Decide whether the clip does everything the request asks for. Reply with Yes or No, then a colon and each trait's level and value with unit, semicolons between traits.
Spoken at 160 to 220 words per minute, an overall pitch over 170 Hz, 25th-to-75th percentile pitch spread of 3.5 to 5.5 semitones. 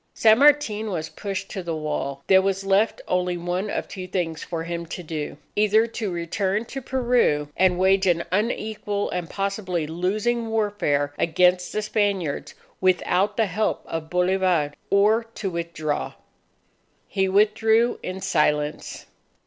No: average, 145 wpm; high, 190 Hz; average, 3.8 semitones